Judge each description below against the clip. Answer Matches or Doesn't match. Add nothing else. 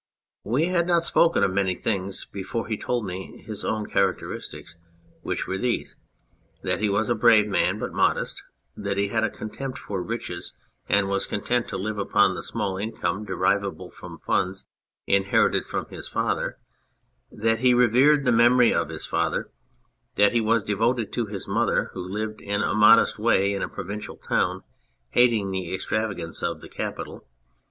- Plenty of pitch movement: Doesn't match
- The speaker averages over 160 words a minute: Matches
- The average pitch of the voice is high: Doesn't match